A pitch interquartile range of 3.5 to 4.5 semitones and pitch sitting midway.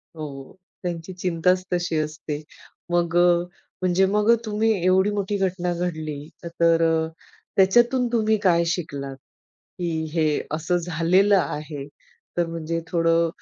No: narrow, 2.4 semitones; medium, 175 Hz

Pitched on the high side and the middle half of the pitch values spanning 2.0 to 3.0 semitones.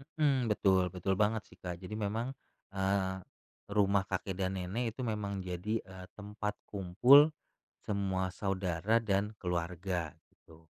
No: low, 100 Hz; narrow, 2.4 semitones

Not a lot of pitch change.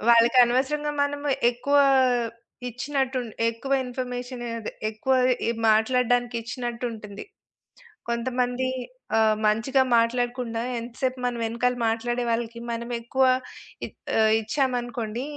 Yes: narrow, 1.8 semitones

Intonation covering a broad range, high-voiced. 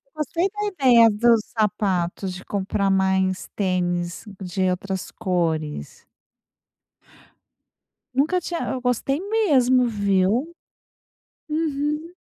Yes: wide, 7.5 semitones; high, 215 Hz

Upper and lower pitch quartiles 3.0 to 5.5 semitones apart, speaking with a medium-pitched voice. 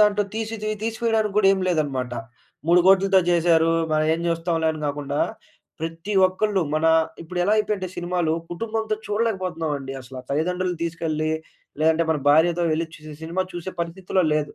Yes: average, 3.5 semitones; medium, 175 Hz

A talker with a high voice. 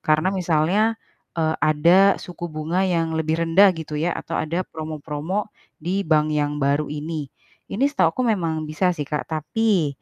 No: medium, 160 Hz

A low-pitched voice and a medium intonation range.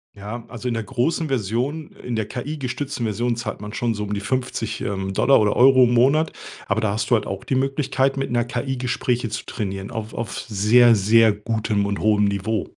Yes: low, 115 Hz; average, 3.5 semitones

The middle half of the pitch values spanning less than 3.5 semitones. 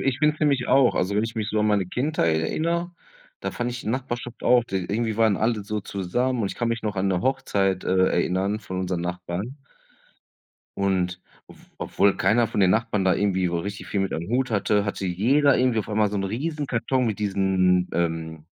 No: average, 4.5 semitones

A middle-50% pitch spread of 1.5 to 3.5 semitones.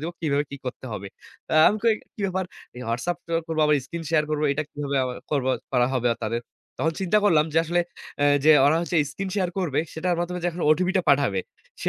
No: average, 3.9 semitones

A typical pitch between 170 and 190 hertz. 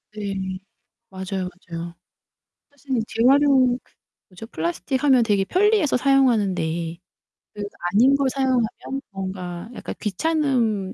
No: high, 225 Hz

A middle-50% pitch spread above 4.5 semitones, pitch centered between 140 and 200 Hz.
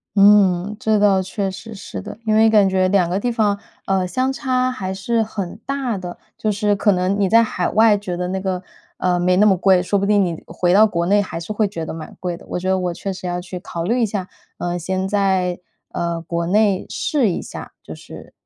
No: average, 2.8 semitones; high, 195 Hz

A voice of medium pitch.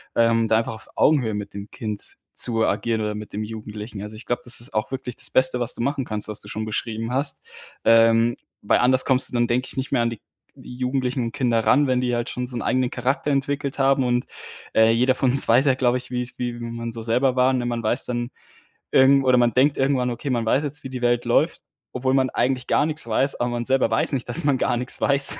No: low, 125 Hz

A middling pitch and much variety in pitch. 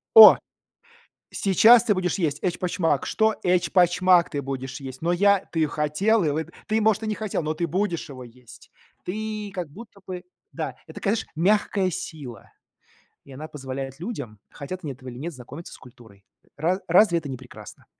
Yes: medium, 170 Hz; wide, 6.1 semitones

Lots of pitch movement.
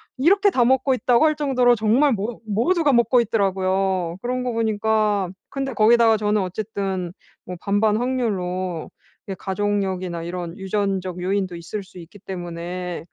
No: average, 4.4 semitones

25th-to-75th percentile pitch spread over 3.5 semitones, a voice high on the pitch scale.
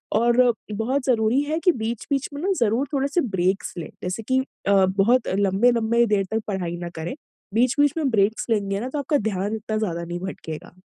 Yes: average, 4.7 semitones; high, 220 Hz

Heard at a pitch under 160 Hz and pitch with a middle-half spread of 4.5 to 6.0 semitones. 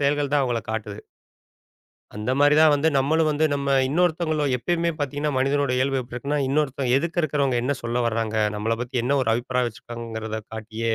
No: low, 135 Hz; average, 3.9 semitones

